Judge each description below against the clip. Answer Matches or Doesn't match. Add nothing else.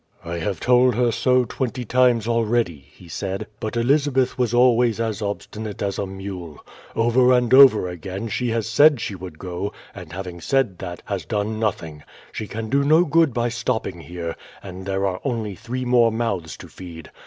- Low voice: Matches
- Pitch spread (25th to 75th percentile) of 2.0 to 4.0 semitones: Doesn't match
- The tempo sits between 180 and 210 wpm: Matches